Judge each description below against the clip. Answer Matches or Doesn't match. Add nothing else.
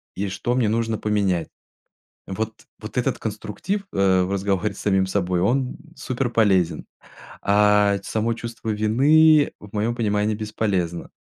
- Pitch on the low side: Matches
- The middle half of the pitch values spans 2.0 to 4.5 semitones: Matches